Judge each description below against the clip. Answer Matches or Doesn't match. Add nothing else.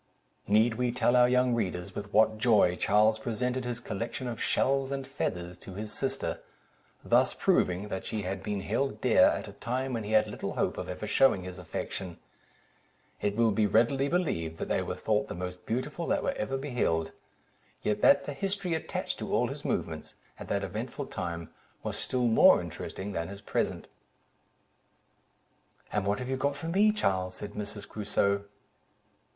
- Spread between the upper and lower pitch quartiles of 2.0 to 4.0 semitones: Doesn't match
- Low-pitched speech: Matches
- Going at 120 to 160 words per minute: Doesn't match